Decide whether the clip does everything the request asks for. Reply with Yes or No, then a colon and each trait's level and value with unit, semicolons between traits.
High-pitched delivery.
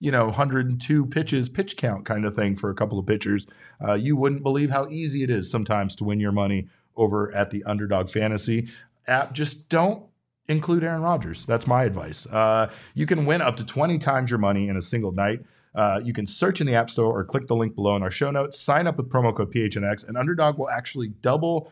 No: low, 120 Hz